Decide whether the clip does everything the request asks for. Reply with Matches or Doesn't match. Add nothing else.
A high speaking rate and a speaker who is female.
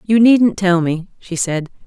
Doesn't match